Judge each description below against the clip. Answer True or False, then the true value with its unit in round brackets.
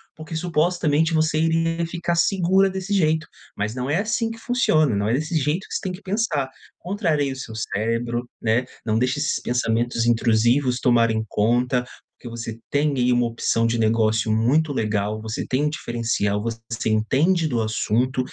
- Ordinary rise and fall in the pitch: False (5.9 semitones)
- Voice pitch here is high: False (125 Hz)